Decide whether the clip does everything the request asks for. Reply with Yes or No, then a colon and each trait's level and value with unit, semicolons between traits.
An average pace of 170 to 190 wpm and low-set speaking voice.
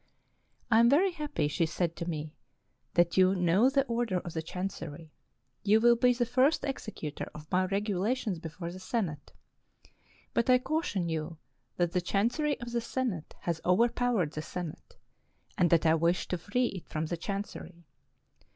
No: average, 175 wpm; medium, 185 Hz